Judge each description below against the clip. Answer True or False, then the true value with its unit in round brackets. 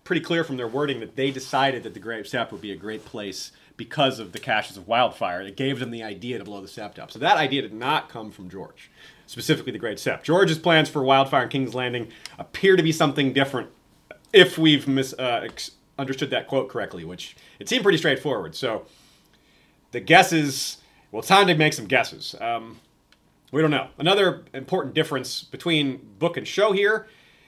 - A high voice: False (135 Hz)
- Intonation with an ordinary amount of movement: True (4.5 semitones)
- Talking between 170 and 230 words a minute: True (205 wpm)